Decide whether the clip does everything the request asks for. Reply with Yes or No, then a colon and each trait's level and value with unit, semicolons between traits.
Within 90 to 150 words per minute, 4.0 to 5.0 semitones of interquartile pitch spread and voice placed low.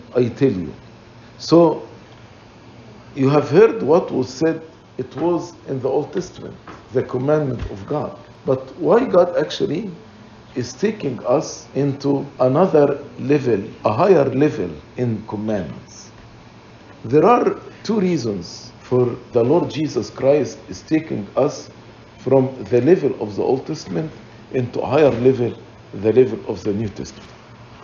Yes: average, 140 wpm; average, 4.6 semitones; low, 130 Hz